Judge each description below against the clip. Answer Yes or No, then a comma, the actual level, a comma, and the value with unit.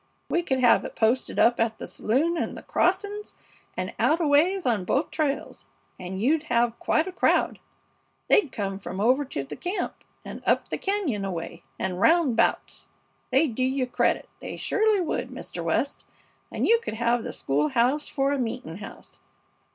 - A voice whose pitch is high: Yes, very high, 255 Hz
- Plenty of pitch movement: Yes, wide, 6.8 semitones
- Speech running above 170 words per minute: Yes, average, 180 wpm